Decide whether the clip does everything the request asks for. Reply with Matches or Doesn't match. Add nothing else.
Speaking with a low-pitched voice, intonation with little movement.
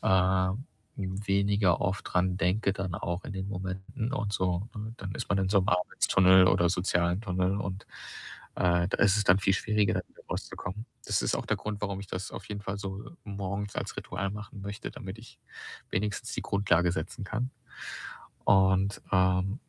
Matches